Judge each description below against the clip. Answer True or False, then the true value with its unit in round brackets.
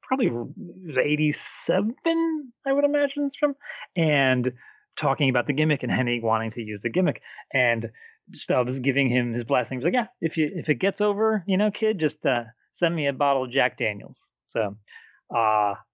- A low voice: False (150 Hz)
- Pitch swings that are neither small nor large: False (8.9 semitones)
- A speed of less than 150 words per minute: False (175 wpm)